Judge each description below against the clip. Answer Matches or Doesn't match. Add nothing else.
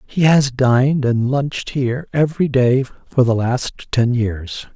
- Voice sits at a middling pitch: Doesn't match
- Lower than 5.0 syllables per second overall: Matches